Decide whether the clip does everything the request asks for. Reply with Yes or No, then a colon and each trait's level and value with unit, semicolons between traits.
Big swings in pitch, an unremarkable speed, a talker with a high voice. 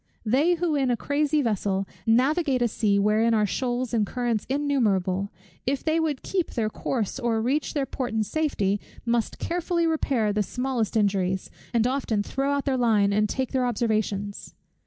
No: average, 4.7 semitones; average, 175 wpm; high, 240 Hz